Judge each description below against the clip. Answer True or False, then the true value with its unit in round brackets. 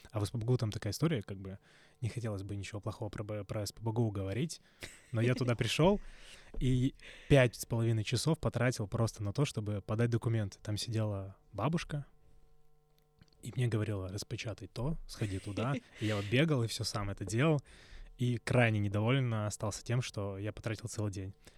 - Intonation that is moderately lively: True (3.7 semitones)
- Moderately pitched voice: False (115 Hz)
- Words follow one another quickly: True (170 wpm)